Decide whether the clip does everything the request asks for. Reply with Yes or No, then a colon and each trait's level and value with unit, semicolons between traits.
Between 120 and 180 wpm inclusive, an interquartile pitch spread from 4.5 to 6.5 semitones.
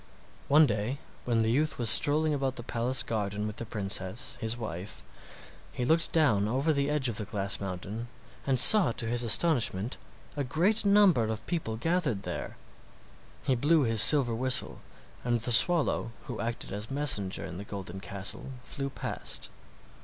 Yes: average, 170 wpm; average, 5.2 semitones